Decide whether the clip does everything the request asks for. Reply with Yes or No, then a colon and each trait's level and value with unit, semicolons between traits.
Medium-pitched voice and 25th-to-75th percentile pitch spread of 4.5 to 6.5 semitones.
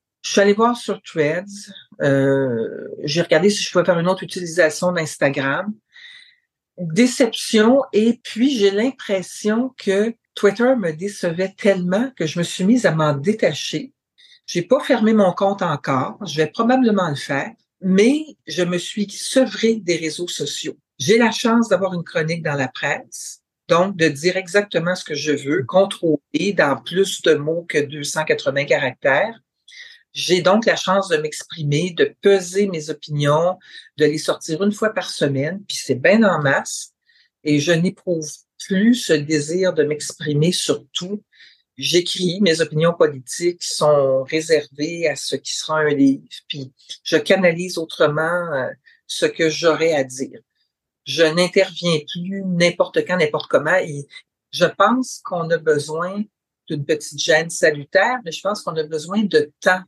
Yes: medium, 180 Hz; average, 4.8 semitones